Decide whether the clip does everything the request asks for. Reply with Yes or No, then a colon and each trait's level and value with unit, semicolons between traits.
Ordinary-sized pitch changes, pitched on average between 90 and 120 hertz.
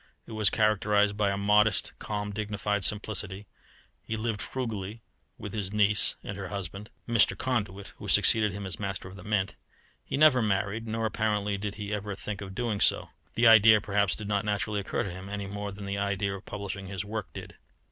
No: narrow, 1.3 semitones; low, 105 Hz